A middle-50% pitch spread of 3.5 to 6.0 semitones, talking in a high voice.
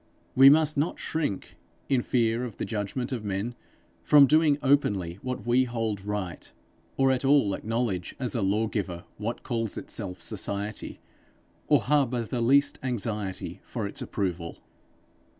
No: average, 4.6 semitones; low, 115 Hz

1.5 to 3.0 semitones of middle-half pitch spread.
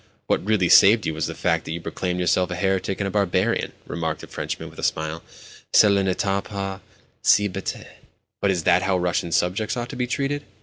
Yes: narrow, 2.6 semitones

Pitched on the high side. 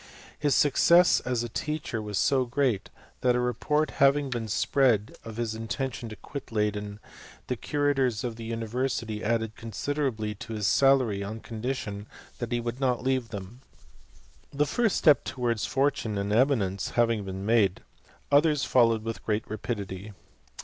No: low, 115 Hz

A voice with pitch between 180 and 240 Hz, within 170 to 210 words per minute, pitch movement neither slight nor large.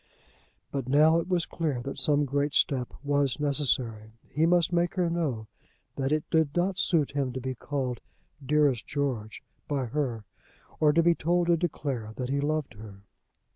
No: medium, 145 Hz; average, 175 wpm; average, 3.8 semitones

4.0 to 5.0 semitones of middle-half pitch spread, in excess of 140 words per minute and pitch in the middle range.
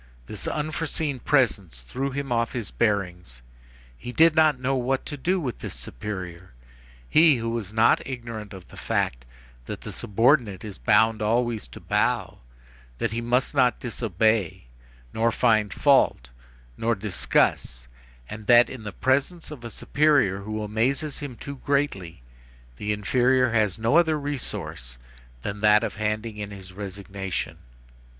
No: average, 4.6 semitones; average, 150 wpm; low, 115 Hz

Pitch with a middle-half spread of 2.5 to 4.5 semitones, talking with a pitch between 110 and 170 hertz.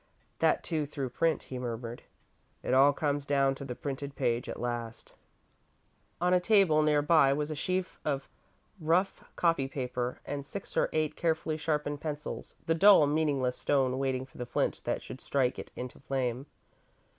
Yes: average, 3.2 semitones; medium, 140 Hz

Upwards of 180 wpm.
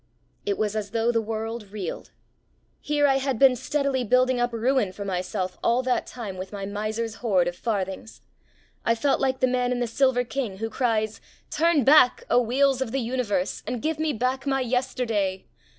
Yes: average, 190 wpm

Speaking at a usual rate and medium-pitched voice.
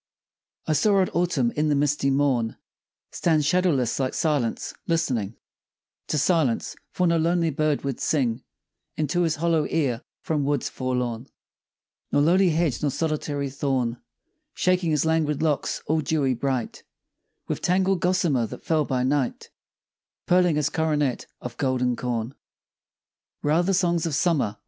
Yes: average, 145 wpm; medium, 150 Hz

